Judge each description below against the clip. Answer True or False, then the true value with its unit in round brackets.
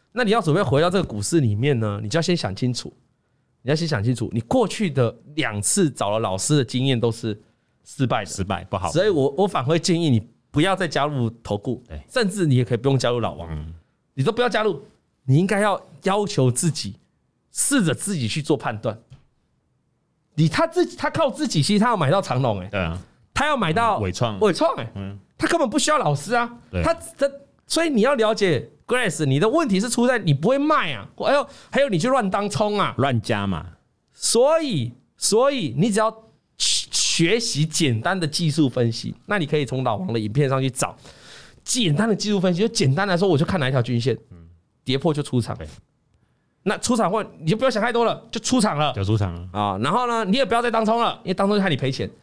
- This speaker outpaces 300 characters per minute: True (315 characters per minute)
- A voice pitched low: False (155 Hz)